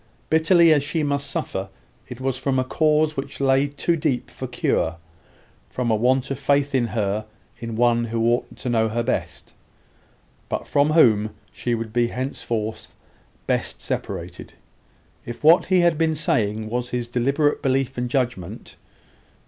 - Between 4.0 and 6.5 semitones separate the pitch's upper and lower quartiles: No, average, 3.6 semitones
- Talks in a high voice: No, low, 130 Hz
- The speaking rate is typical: Yes, average, 160 wpm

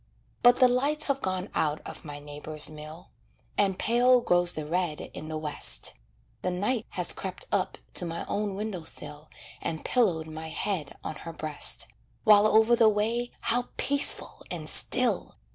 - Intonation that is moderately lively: No, wide, 6.7 semitones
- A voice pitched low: No, medium, 185 Hz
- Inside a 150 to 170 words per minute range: Yes, average, 165 wpm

